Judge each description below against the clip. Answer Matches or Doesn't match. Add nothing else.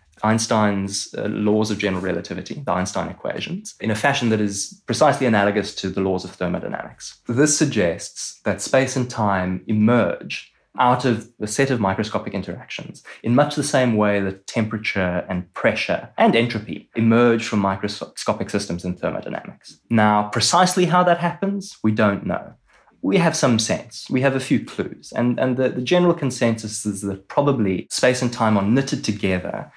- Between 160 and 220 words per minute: Matches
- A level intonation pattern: Doesn't match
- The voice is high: Doesn't match